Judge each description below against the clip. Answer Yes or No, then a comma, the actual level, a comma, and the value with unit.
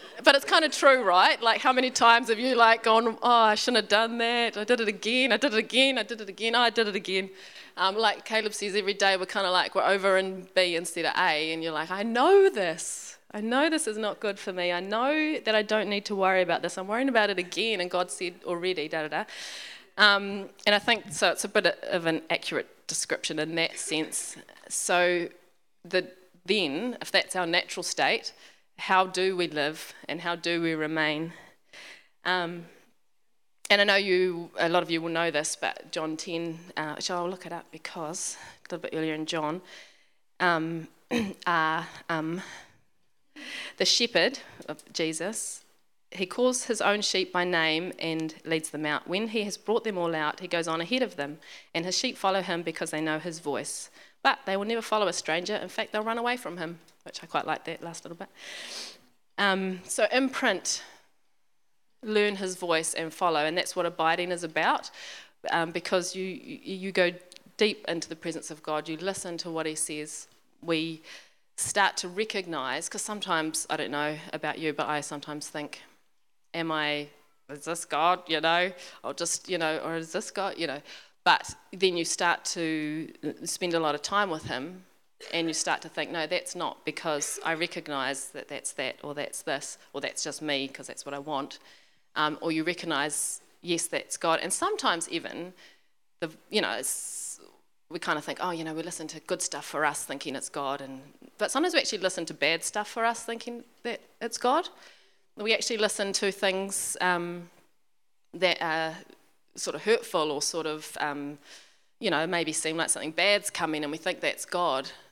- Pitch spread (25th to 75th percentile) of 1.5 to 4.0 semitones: No, average, 4.6 semitones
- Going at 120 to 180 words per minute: No, average, 200 wpm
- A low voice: No, medium, 180 Hz